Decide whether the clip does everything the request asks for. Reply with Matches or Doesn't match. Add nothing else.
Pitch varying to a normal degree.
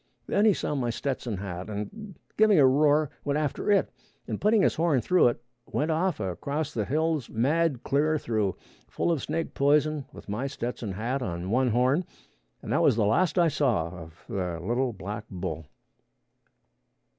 Doesn't match